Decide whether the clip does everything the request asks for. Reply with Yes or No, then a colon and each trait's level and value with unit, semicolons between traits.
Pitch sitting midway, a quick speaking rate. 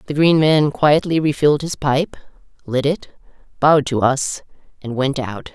No: medium, 145 Hz; average, 160 wpm